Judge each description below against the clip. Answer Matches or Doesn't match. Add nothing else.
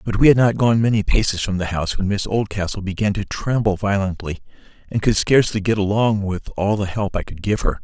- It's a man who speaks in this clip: Matches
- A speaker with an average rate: Doesn't match